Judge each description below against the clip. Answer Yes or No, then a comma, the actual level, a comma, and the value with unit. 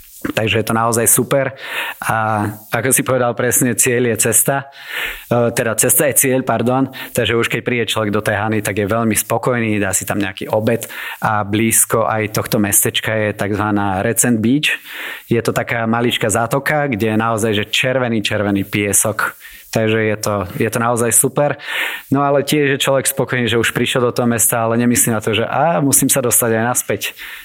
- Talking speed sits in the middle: No, fast, 190 wpm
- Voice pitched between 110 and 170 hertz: Yes, low, 115 Hz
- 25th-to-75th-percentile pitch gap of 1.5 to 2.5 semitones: No, average, 2.9 semitones